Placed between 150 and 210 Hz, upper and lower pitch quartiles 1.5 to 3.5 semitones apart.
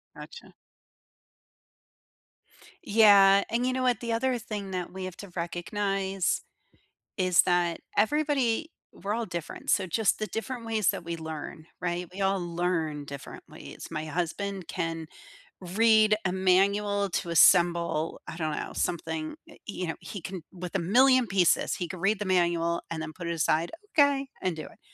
No: medium, 185 Hz; average, 3.9 semitones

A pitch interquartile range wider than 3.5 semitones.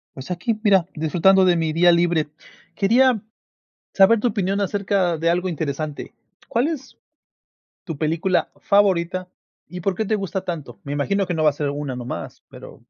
Yes: average, 3.9 semitones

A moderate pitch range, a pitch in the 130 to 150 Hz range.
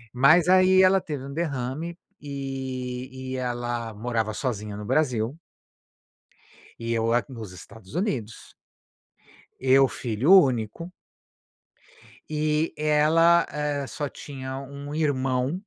Yes: average, 3.9 semitones; low, 135 Hz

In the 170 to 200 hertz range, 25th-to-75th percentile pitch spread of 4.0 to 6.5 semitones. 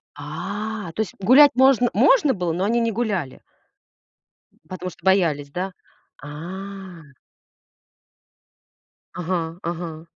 Yes: medium, 185 Hz; average, 4.8 semitones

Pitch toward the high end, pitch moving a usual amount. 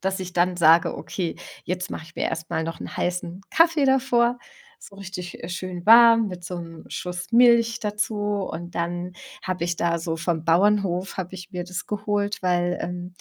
No: medium, 180 Hz; average, 3.0 semitones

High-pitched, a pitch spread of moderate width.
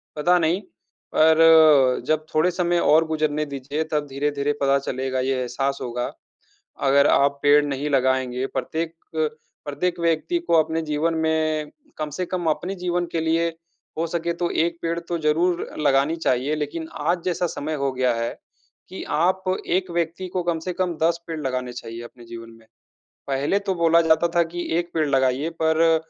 No: medium, 155 Hz; average, 3.4 semitones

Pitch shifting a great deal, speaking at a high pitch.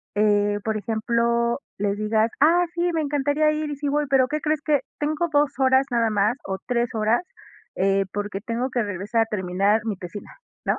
Yes: wide, 5.8 semitones; high, 235 Hz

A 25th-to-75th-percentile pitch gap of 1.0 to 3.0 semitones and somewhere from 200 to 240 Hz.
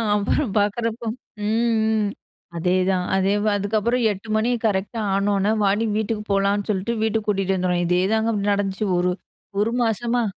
Yes: narrow, 2.5 semitones; high, 205 Hz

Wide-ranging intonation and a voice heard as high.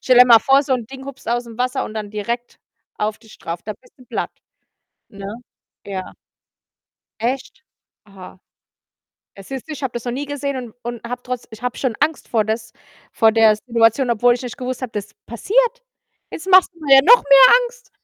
No: average, 3.4 semitones; high, 245 Hz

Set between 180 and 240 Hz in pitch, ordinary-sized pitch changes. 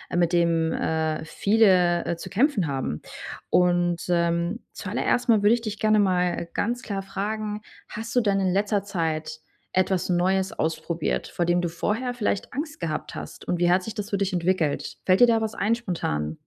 Yes: medium, 185 Hz; average, 3.8 semitones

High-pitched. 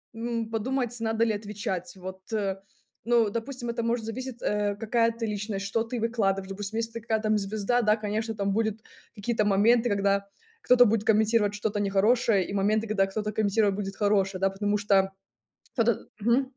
Yes: high, 215 Hz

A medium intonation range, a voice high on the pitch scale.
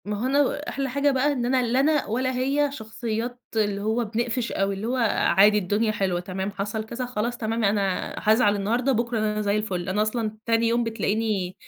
Yes: average, 3.1 semitones; high, 225 Hz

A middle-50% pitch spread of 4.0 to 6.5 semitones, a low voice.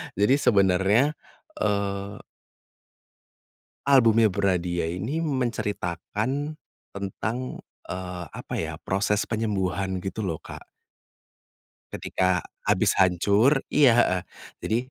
Yes: average, 4.3 semitones; low, 100 Hz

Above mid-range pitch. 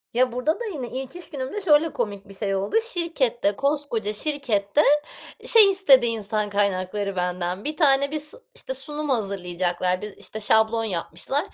Yes: high, 235 Hz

